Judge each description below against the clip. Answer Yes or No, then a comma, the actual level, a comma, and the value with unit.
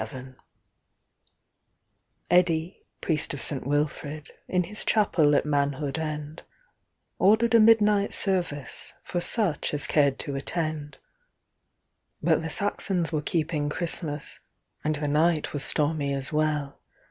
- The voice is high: No, medium, 155 Hz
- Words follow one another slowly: Yes, slow, 100 wpm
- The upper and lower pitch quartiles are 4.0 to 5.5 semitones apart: No, average, 3.5 semitones